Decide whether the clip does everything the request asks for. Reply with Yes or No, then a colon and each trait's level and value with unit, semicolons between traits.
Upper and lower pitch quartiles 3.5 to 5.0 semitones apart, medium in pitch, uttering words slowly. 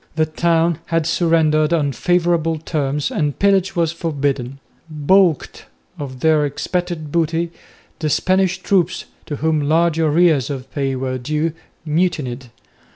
No: average, 2.9 semitones; medium, 155 Hz; slow, 130 wpm